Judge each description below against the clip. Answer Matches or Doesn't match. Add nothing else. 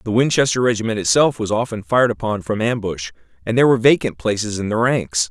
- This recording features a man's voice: Matches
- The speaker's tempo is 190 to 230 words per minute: Matches